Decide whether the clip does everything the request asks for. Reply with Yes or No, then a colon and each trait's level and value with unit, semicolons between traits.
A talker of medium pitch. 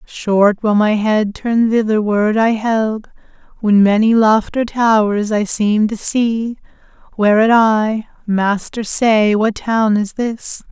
No: high, 215 Hz